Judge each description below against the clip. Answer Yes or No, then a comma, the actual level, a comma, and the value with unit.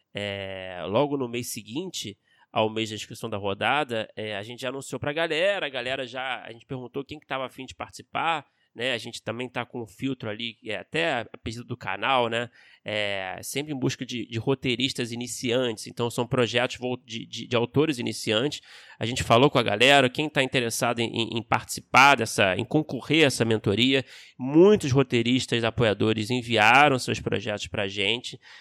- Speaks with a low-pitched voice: Yes, low, 120 Hz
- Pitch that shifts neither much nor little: Yes, average, 3.1 semitones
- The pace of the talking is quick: Yes, fast, 190 wpm